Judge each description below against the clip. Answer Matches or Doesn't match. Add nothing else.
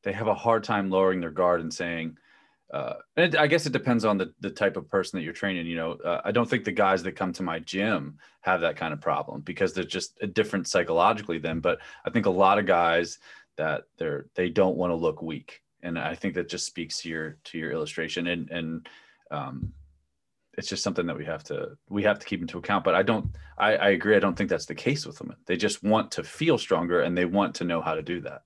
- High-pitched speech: Doesn't match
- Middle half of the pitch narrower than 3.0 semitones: Doesn't match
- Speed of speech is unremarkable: Doesn't match